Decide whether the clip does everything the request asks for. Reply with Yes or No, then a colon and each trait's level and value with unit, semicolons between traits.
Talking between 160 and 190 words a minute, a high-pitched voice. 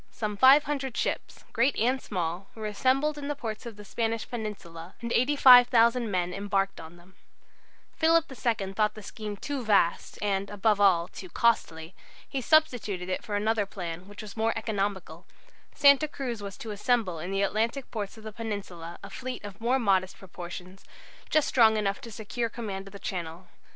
Yes: average, 180 wpm; high, 210 Hz